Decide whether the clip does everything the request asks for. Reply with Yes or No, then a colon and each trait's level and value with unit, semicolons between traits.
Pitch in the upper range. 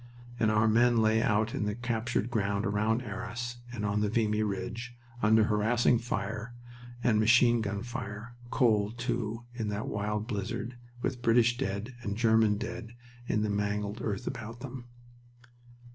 No: low, 110 Hz